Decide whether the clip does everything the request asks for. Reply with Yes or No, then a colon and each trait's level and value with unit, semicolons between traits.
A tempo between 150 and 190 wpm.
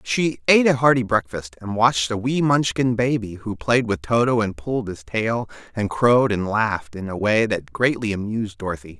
No: average, 200 wpm